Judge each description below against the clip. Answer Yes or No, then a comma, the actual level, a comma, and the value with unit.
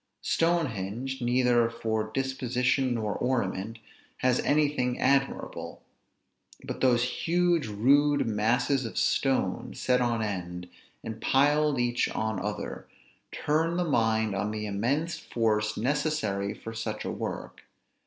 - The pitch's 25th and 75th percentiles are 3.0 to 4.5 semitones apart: Yes, average, 4.0 semitones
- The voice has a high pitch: No, low, 120 Hz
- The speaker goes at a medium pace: No, slow, 120 wpm